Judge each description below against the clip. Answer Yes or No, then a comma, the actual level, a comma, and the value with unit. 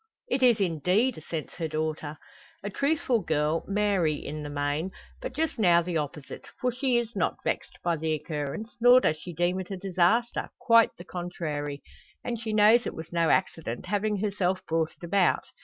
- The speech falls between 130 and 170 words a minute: No, average, 185 wpm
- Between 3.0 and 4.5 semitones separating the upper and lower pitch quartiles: No, wide, 5.5 semitones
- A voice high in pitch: No, medium, 180 Hz